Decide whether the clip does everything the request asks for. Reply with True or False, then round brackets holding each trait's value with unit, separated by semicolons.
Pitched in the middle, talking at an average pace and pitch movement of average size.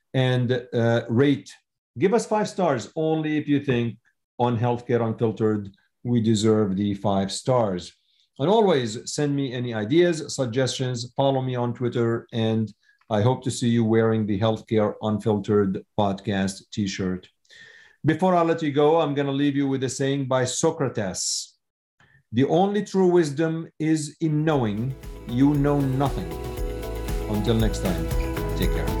False (125 Hz; 150 wpm; 4.7 semitones)